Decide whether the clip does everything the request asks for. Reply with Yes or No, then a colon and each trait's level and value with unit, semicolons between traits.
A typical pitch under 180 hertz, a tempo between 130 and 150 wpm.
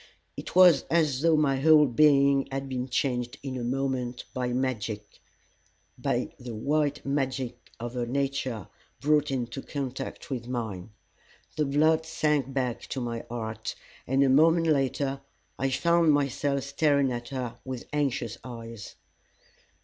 Yes: low, 135 Hz; average, 140 wpm